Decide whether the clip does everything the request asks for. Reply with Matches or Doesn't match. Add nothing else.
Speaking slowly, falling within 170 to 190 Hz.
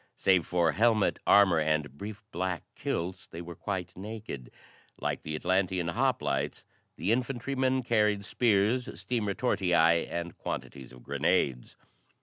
Doesn't match